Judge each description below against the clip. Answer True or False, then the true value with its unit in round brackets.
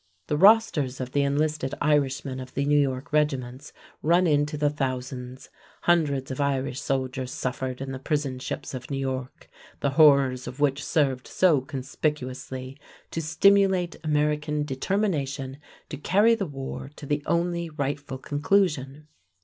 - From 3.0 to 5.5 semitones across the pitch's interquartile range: False (2.5 semitones)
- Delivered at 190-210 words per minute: False (145 wpm)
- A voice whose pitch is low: False (145 Hz)